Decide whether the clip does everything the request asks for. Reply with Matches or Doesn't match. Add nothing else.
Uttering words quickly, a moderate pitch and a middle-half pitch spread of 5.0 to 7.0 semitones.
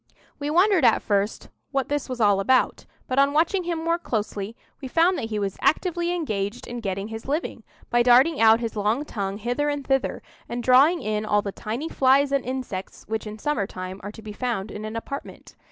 Doesn't match